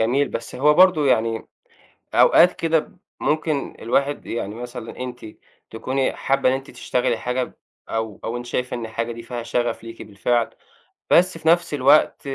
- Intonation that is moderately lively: Yes, average, 3.8 semitones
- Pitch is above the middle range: No, low, 125 Hz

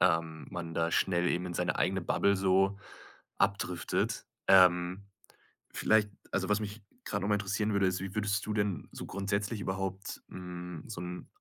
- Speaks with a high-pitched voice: No, very low, 95 Hz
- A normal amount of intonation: No, narrow, 2.2 semitones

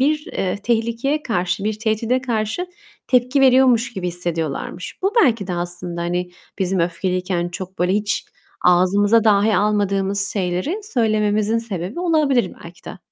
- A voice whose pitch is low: No, high, 205 Hz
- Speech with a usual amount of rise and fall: Yes, average, 4.7 semitones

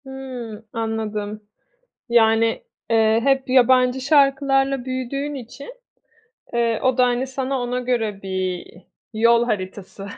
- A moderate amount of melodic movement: Yes, average, 3.1 semitones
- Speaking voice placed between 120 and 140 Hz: No, high, 240 Hz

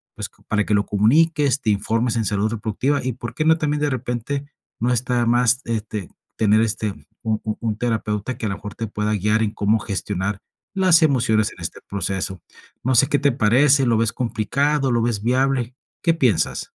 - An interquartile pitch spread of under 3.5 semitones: No, average, 3.8 semitones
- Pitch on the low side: Yes, low, 115 Hz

